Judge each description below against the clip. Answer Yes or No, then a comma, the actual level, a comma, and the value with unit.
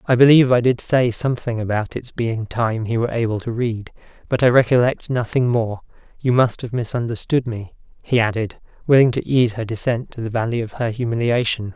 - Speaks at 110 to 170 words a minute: No, average, 190 wpm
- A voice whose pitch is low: Yes, low, 120 Hz